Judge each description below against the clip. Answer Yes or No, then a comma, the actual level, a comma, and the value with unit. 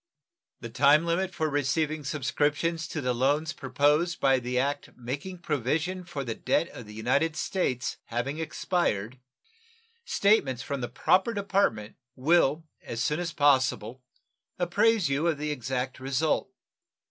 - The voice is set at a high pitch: No, medium, 145 Hz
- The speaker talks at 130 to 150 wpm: Yes, average, 140 wpm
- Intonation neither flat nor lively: Yes, average, 4.5 semitones